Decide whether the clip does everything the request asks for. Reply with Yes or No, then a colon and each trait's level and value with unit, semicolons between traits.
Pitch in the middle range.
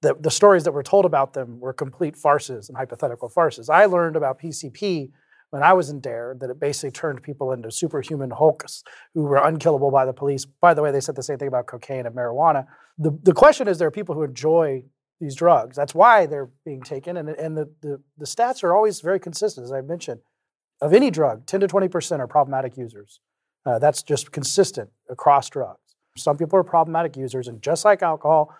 Yes: medium, 150 Hz